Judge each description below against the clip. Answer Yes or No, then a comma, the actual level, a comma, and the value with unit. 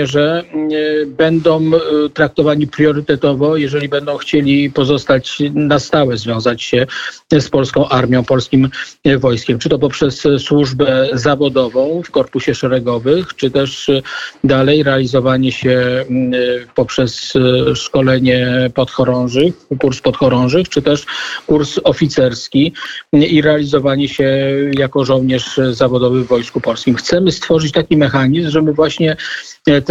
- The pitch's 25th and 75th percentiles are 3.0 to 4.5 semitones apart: No, narrow, 2.6 semitones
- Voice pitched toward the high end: No, medium, 140 Hz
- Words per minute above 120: No, slow, 110 wpm